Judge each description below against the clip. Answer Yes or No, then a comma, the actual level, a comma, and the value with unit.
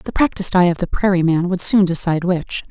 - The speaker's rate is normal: No, fast, 245 wpm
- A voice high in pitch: No, medium, 180 Hz